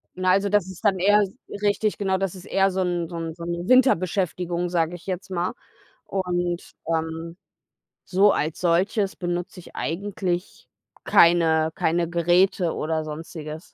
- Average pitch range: No, narrow, 2.3 semitones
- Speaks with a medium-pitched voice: Yes, medium, 175 Hz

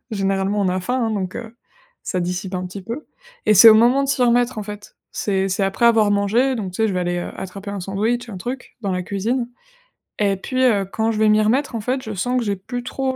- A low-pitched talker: No, high, 210 Hz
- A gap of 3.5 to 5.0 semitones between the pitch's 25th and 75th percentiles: Yes, average, 3.9 semitones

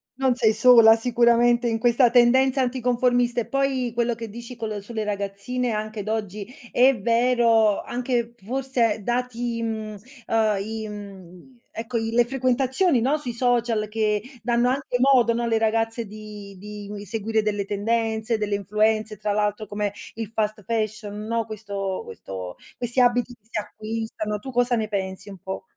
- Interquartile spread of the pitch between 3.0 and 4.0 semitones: No, narrow, 2.4 semitones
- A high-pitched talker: Yes, high, 225 Hz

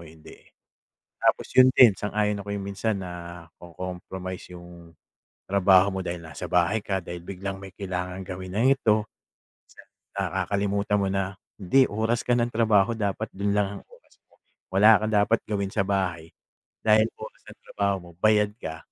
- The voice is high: No, low, 100 Hz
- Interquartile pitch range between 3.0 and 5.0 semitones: No, narrow, 2.5 semitones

